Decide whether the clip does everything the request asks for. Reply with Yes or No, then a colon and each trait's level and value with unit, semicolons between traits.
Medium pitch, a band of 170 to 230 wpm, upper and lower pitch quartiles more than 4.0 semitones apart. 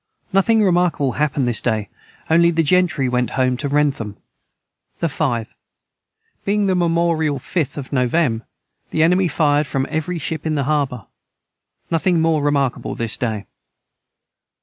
No: medium, 150 Hz; average, 140 wpm; average, 4.6 semitones